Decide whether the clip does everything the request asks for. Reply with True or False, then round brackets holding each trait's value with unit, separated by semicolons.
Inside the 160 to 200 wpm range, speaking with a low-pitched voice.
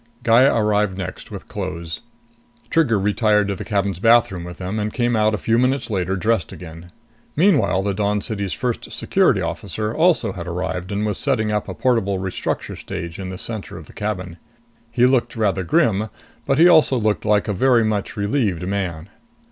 True (185 wpm; 105 Hz)